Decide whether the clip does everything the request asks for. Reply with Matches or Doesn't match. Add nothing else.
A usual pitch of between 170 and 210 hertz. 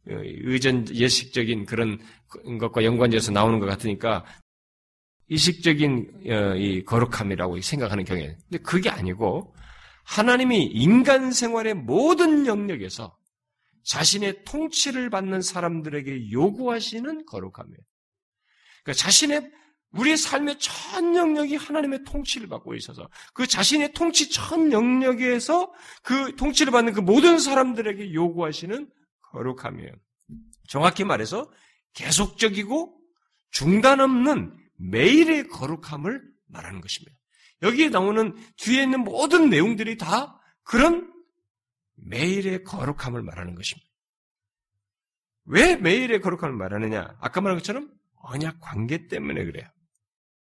Matches